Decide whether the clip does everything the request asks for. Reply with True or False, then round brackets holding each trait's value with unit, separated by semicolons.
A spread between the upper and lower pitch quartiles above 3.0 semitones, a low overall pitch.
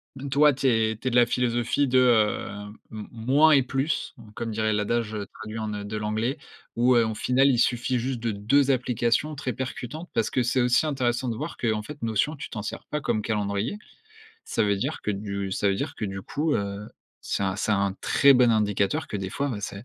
True (3.7 semitones; 115 Hz)